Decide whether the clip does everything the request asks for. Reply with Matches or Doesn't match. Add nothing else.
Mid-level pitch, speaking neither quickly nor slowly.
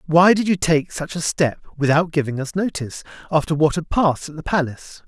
Doesn't match